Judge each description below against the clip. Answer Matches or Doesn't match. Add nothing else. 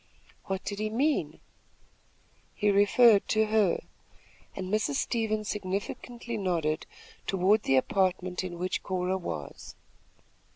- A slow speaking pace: Matches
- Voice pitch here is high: Matches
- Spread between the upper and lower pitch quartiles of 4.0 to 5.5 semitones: Doesn't match